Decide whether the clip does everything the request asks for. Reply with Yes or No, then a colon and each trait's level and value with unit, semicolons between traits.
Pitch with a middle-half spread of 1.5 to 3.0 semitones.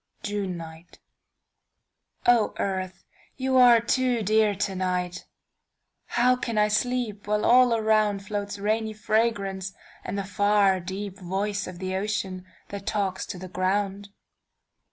Yes: narrow, 2.4 semitones